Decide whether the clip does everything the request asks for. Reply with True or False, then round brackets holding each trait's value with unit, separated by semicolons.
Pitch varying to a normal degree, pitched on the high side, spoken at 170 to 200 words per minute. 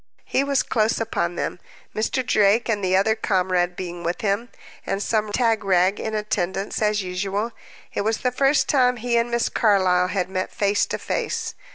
True (3.4 semitones; 210 Hz; 180 wpm)